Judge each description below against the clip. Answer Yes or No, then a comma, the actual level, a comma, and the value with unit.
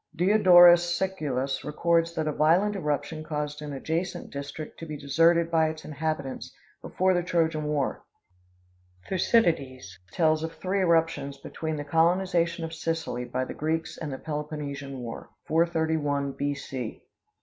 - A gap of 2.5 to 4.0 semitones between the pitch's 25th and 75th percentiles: Yes, average, 2.8 semitones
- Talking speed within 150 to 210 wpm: No, average, 140 wpm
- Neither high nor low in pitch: Yes, medium, 160 Hz